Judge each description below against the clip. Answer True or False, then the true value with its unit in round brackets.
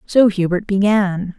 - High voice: True (195 Hz)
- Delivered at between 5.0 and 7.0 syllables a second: False (3.9 syllables/s)